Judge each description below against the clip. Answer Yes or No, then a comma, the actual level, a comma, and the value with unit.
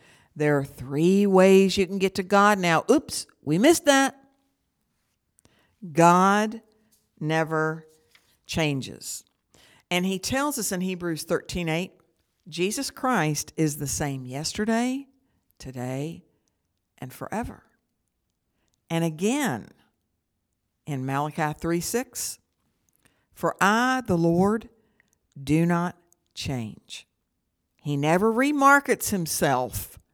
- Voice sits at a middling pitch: Yes, medium, 175 Hz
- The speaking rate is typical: No, slow, 100 wpm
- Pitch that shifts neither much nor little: No, wide, 5.9 semitones